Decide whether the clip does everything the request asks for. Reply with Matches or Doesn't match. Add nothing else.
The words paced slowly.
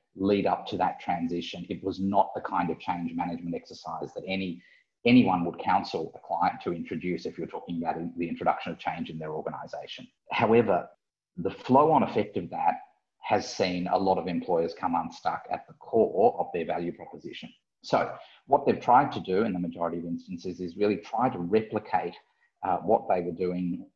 Doesn't match